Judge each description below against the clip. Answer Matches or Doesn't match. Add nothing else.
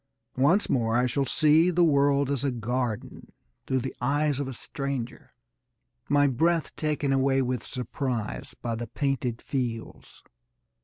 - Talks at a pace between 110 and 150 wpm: Matches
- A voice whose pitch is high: Doesn't match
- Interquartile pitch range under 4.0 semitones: Matches